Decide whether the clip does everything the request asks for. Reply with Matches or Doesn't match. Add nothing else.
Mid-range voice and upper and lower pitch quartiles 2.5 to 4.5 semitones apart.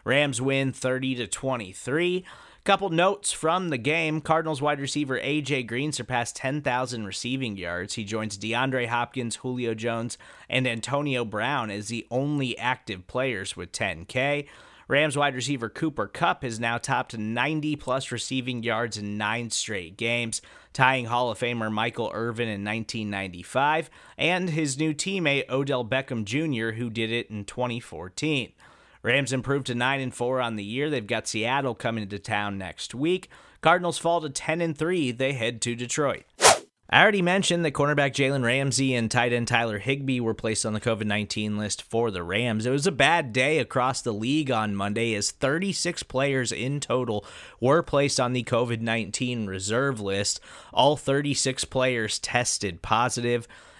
Doesn't match